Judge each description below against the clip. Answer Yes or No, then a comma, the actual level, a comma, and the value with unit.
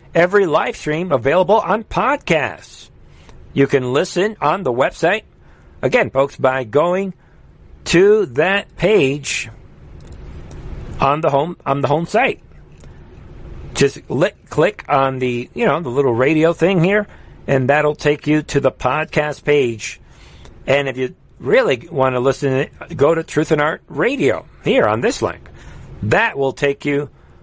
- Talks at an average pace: Yes, average, 145 wpm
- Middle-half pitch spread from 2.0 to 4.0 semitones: No, average, 5.1 semitones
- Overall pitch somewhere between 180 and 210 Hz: No, medium, 140 Hz